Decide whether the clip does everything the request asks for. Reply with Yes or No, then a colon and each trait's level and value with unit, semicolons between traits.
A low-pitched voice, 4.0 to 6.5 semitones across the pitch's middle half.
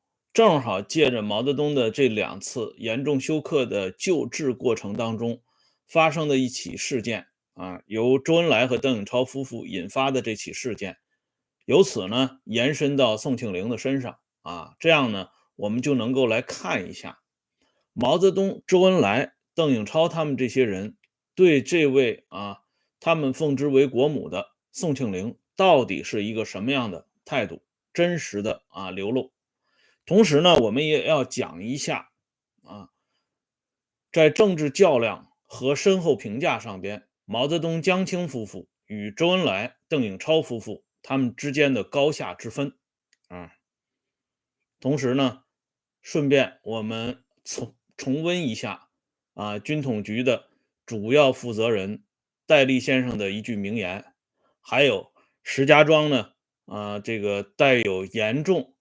Yes: low, 130 Hz; average, 5.1 semitones